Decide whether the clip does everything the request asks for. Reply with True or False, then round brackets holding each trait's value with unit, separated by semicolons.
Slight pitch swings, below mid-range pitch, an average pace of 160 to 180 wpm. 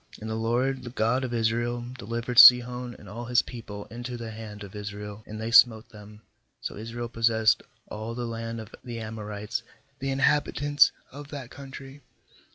True (2.1 semitones; 115 Hz; 175 wpm)